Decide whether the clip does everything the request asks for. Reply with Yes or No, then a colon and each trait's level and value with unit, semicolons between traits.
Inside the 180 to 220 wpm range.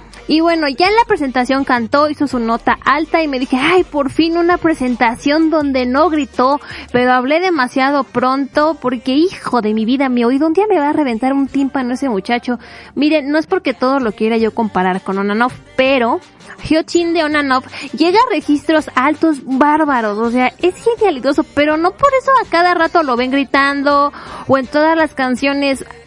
Yes: fast, 190 wpm